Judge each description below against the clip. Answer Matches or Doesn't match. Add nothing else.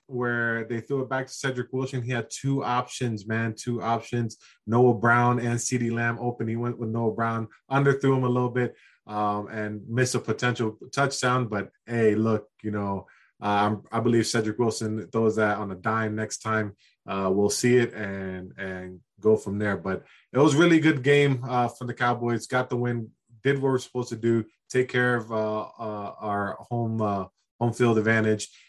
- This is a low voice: Matches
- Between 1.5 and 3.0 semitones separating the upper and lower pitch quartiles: Matches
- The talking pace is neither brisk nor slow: Matches